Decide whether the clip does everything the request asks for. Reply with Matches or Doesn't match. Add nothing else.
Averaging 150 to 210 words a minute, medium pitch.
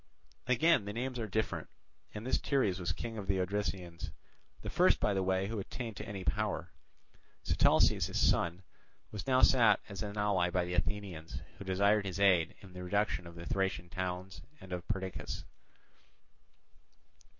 Doesn't match